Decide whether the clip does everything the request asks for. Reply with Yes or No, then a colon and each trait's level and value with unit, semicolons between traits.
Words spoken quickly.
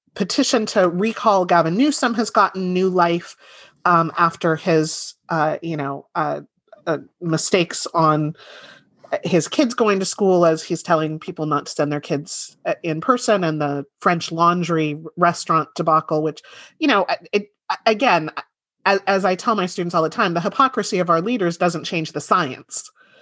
No: average, 165 wpm